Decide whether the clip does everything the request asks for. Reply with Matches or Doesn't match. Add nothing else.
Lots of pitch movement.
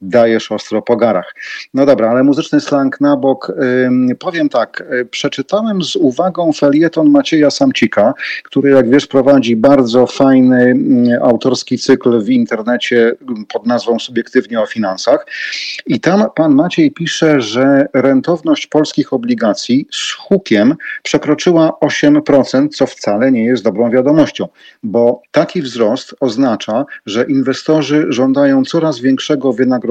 Doesn't match